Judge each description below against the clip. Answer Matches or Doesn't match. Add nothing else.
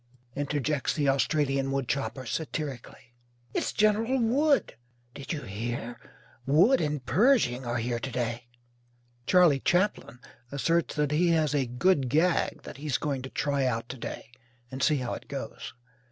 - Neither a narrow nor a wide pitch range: Matches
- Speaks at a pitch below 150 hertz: Matches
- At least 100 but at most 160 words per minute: Matches